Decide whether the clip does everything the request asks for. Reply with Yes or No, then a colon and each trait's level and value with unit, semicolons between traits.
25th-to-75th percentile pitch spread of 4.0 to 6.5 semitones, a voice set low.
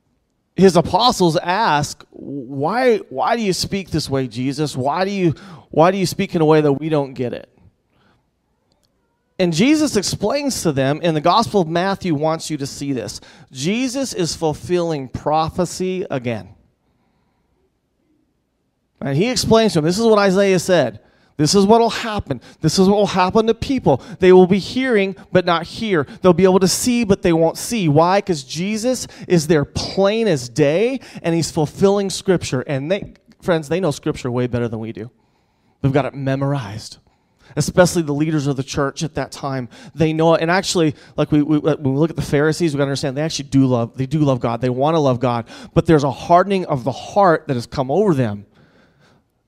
No: average, 5.3 semitones; medium, 160 Hz